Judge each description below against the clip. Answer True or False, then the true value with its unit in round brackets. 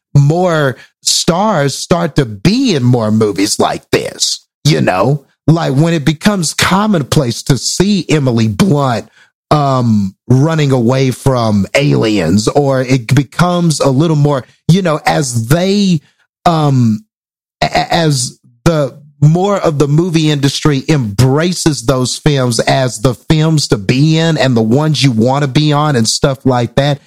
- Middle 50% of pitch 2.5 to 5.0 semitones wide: True (3.9 semitones)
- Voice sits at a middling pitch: True (145 Hz)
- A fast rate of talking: False (145 wpm)